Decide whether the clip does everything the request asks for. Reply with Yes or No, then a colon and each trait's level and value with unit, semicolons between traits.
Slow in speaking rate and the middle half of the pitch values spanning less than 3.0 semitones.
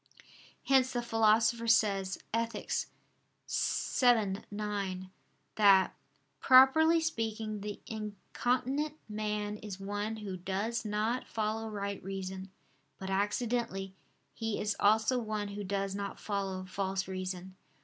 Yes: slow, 110 wpm; narrow, 2.6 semitones